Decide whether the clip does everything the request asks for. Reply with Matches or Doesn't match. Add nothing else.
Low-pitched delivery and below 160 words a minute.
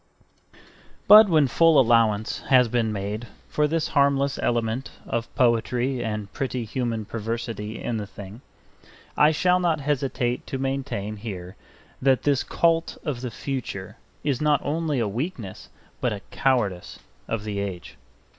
Matches